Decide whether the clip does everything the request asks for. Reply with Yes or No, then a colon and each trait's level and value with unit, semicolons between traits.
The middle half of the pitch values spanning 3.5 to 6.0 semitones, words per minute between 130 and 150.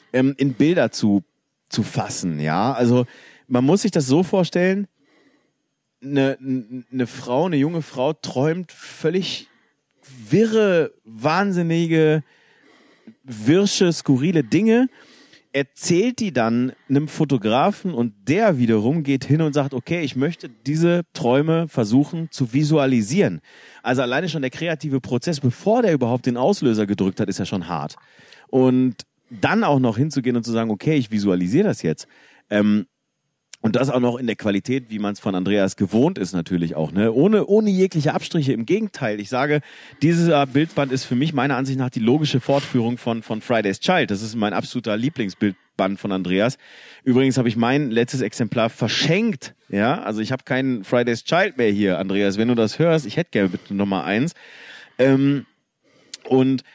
No: average, 5.3 semitones; average, 160 wpm